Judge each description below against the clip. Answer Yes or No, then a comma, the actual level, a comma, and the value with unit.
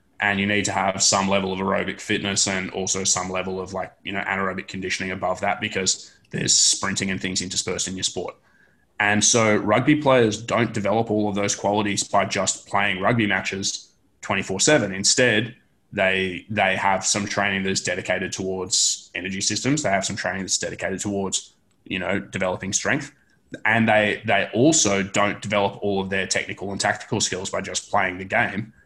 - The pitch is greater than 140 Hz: No, low, 100 Hz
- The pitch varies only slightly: Yes, narrow, 1.6 semitones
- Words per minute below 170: No, average, 185 wpm